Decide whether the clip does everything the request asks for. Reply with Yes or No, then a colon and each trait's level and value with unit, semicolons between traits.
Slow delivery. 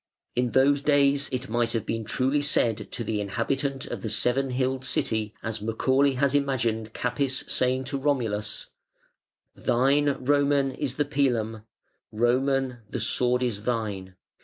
No: average, 155 wpm